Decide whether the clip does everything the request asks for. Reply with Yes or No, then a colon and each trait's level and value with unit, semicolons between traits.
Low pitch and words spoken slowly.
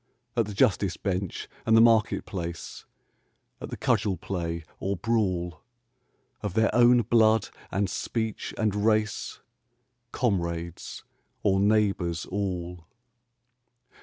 Yes: low, 100 Hz; slow, 110 wpm